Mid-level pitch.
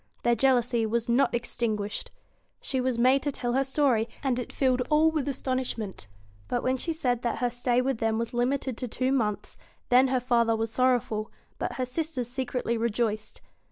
No: high, 245 Hz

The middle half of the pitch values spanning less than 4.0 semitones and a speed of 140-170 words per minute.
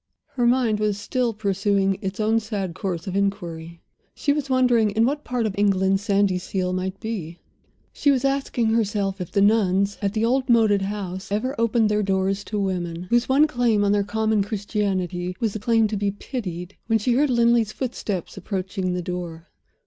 No: average, 3.2 semitones; average, 185 wpm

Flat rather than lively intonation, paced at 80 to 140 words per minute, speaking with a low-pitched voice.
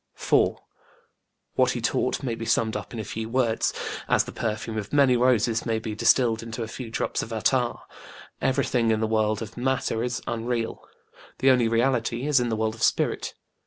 No: narrow, 1.9 semitones; average, 195 wpm; low, 115 Hz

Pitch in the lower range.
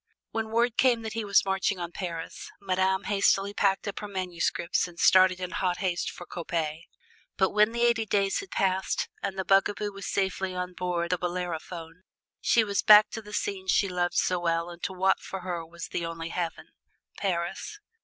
No: high, 190 Hz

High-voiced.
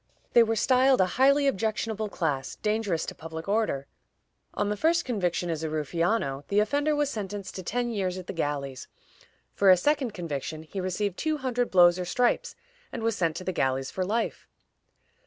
Yes: high, 200 Hz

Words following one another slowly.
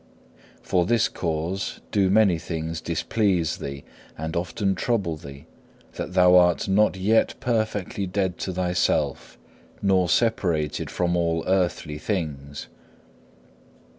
Yes: slow, 115 wpm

